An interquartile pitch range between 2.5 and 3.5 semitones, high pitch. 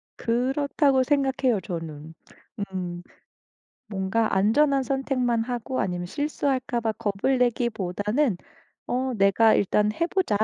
No: average, 5.2 semitones; high, 235 Hz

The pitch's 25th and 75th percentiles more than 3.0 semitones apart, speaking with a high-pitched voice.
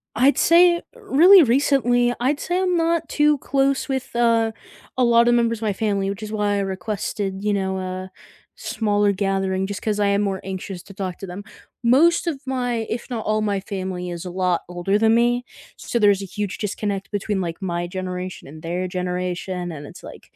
Yes: average, 4.4 semitones; high, 205 Hz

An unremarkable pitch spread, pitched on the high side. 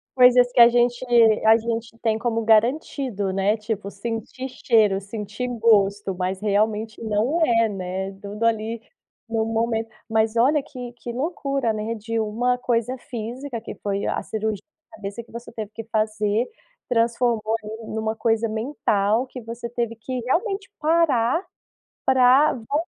No: narrow, 2.3 semitones; high, 230 Hz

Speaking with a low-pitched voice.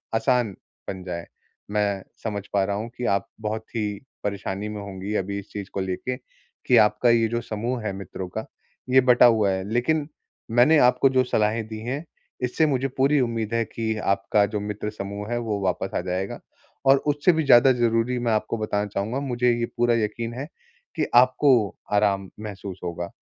Yes: low, 110 Hz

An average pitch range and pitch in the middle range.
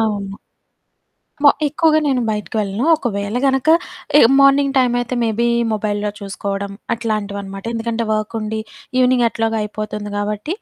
No: average, 3.0 semitones; high, 220 Hz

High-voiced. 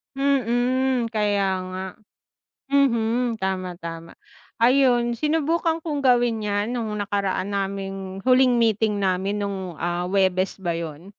Yes: high, 210 Hz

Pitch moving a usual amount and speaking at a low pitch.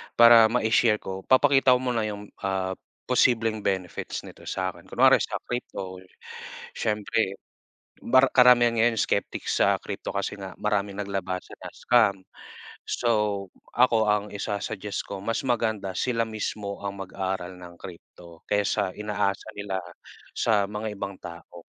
Yes: average, 3.0 semitones; low, 105 Hz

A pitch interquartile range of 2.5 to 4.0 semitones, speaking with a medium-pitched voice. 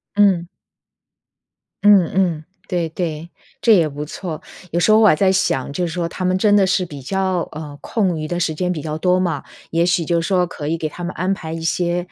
Yes: average, 2.8 semitones; medium, 175 Hz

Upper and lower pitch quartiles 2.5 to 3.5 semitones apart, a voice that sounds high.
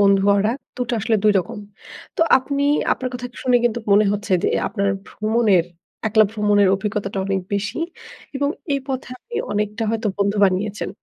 Yes: average, 3.1 semitones; high, 210 Hz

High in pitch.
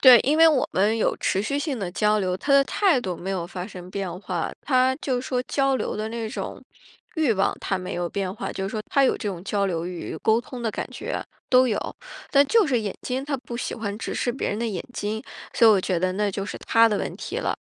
Yes: high, 215 Hz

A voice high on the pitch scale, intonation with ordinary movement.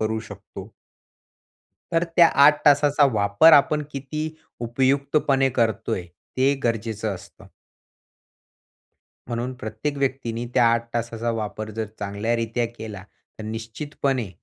No: low, 115 Hz; average, 4.1 semitones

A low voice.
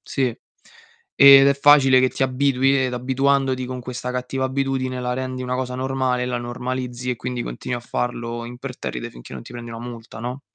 Yes: low, 125 Hz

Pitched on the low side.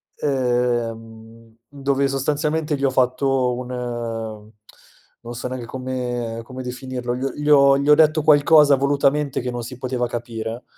Yes: low, 130 Hz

